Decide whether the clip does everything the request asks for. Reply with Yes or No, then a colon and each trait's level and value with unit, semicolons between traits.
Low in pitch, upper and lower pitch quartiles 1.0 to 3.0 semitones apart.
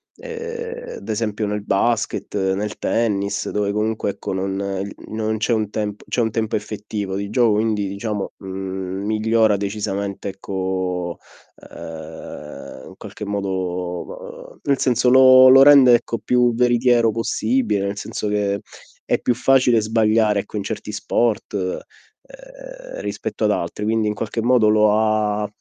Yes: low, 105 Hz; narrow, 2.6 semitones